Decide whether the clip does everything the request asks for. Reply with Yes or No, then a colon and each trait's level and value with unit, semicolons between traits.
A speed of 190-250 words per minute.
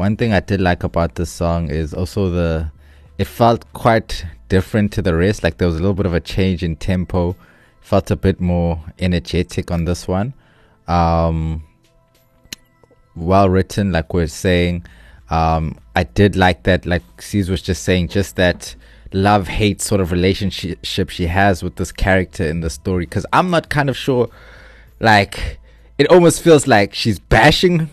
No: average, 170 wpm